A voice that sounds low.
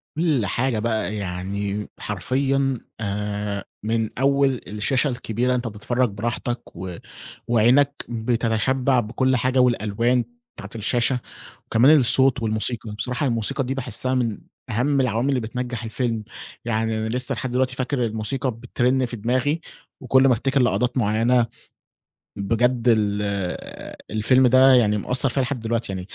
Yes: low, 120 Hz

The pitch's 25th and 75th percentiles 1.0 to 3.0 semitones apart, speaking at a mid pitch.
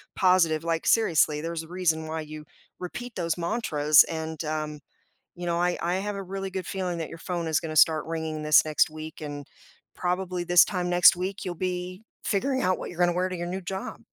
Yes: narrow, 2.6 semitones; medium, 175 Hz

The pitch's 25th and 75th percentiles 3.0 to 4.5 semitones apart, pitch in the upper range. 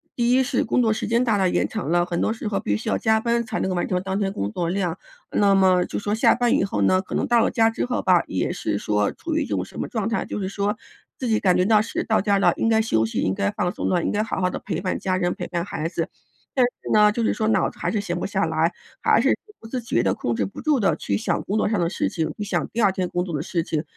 Yes: average, 4.0 semitones; high, 195 Hz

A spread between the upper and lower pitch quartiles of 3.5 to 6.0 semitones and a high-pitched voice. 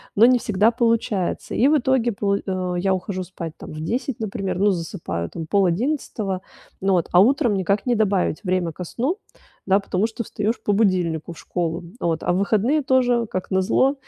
Yes: average, 4.3 semitones; high, 195 Hz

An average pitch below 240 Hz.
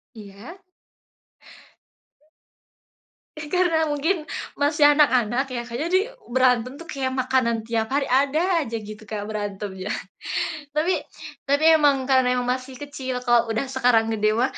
No: very high, 255 Hz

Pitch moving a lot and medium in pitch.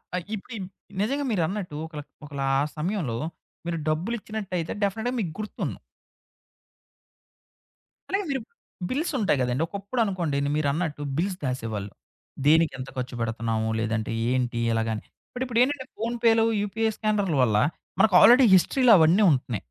Yes: wide, 9.0 semitones; medium, 175 Hz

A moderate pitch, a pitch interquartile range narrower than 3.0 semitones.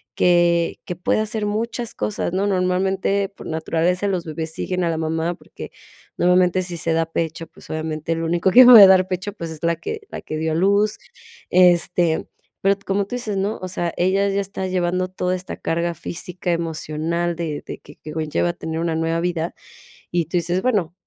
Yes: medium, 175 Hz; narrow, 2.6 semitones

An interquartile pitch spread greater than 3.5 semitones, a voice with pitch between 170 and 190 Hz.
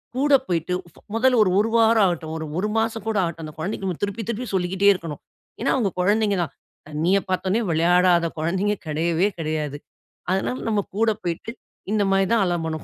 Yes: average, 4.3 semitones; medium, 185 Hz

